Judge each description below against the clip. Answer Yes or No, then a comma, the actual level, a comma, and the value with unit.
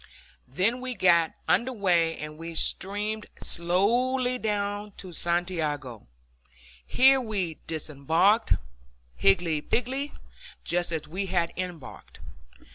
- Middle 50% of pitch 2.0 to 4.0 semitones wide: No, average, 4.9 semitones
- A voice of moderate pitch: Yes, medium, 180 Hz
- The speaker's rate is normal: No, slow, 110 wpm